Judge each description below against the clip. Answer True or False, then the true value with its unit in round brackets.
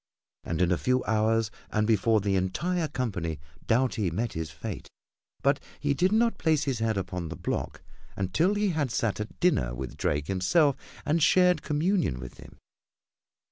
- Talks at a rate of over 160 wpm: True (170 wpm)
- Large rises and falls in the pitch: True (8.7 semitones)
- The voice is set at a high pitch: False (115 Hz)